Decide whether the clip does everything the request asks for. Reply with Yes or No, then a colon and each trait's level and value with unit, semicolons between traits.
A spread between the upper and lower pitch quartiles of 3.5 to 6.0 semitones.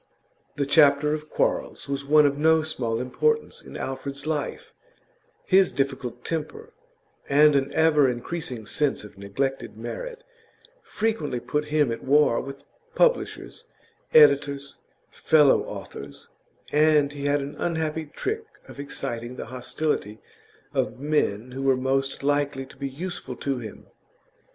No: narrow, 2.6 semitones